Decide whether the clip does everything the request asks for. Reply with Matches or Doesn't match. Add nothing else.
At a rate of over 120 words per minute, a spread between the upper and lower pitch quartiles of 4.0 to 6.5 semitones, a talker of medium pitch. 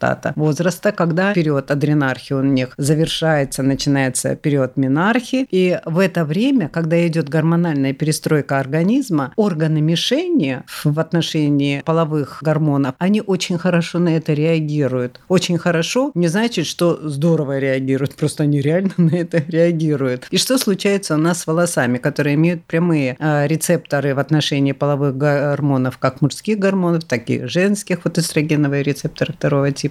Doesn't match